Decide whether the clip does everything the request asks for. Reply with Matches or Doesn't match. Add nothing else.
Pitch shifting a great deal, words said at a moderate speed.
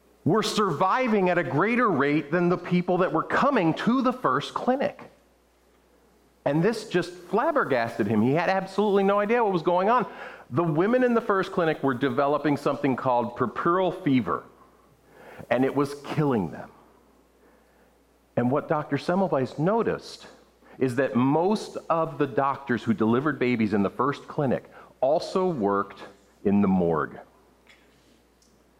Matches